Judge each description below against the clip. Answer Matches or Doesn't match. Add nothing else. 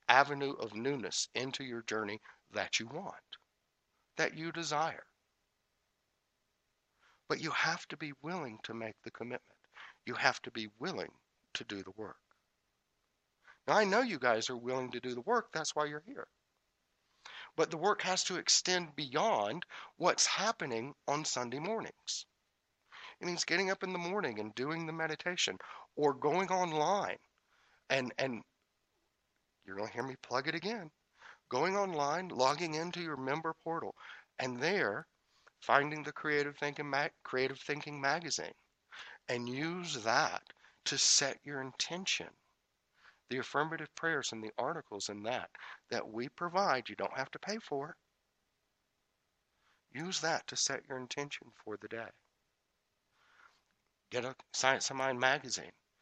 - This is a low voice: Doesn't match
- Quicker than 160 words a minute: Doesn't match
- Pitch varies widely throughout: Doesn't match